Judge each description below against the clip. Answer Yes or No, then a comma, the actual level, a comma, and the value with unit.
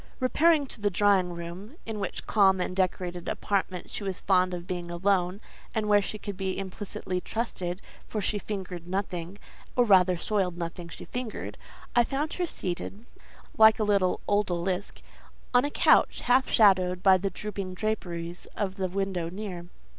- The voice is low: No, high, 190 Hz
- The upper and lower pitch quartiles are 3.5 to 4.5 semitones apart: No, average, 2.8 semitones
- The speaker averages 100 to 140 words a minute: No, average, 160 wpm